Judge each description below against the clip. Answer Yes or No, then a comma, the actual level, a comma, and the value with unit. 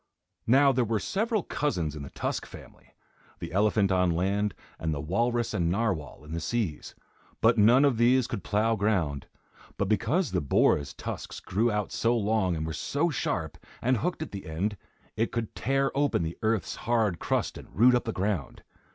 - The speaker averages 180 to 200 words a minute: Yes, average, 185 wpm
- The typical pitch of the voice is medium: No, low, 105 Hz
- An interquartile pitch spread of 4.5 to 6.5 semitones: Yes, average, 5.1 semitones